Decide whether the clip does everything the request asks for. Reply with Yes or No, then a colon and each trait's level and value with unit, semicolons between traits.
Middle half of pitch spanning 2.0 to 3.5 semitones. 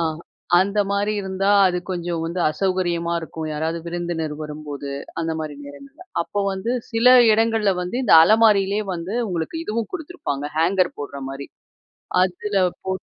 No: average, 4.3 semitones